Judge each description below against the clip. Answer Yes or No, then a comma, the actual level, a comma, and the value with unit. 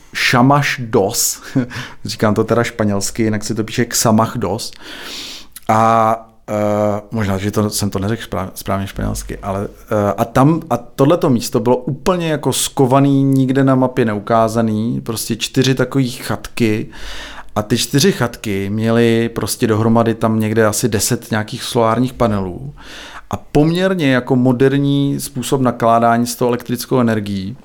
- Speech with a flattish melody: No, average, 3.1 semitones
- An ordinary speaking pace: Yes, average, 140 wpm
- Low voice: Yes, low, 115 Hz